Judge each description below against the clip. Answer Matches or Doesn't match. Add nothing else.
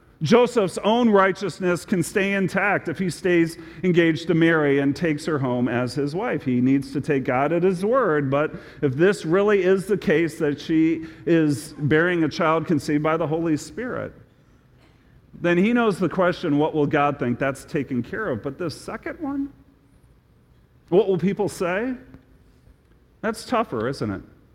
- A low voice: Doesn't match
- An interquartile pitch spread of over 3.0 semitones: Matches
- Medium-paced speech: Matches